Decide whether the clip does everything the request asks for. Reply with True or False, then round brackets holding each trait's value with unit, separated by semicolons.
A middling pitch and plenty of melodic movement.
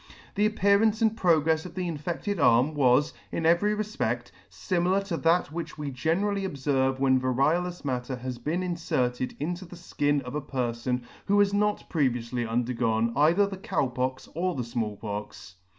True (150 Hz; 6.3 semitones)